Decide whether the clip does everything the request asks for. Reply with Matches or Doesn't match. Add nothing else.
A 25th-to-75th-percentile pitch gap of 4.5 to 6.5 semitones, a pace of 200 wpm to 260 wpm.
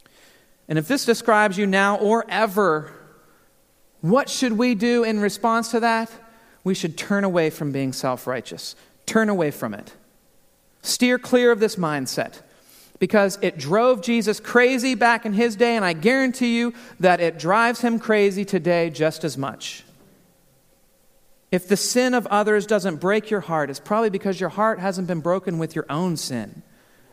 Doesn't match